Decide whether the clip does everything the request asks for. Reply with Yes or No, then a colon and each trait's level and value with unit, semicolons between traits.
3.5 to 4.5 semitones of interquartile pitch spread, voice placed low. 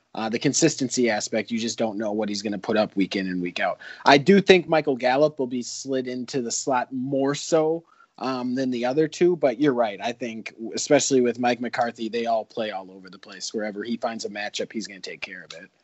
Yes: average, 3.8 semitones; low, 125 Hz